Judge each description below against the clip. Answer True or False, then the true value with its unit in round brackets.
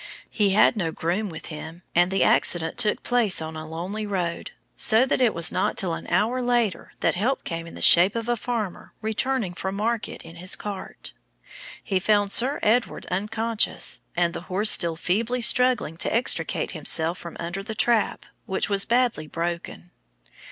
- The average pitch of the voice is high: True (195 Hz)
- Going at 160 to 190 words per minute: True (180 wpm)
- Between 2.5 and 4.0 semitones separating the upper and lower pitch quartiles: False (4.9 semitones)